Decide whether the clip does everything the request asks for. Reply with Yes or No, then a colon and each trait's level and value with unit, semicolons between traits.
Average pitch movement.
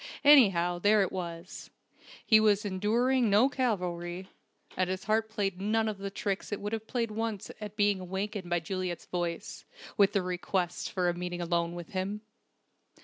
Yes: average, 3.2 semitones